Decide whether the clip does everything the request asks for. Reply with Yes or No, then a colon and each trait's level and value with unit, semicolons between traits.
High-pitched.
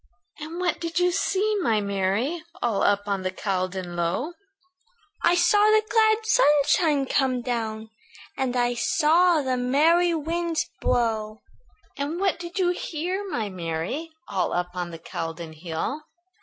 Yes: very high, 265 Hz